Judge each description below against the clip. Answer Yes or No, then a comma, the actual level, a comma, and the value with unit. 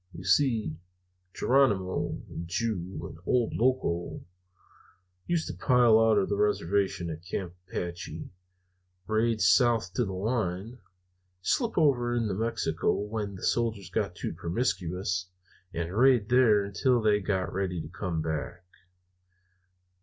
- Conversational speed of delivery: No, slow, 130 wpm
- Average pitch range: Yes, average, 4.5 semitones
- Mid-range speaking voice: No, low, 100 Hz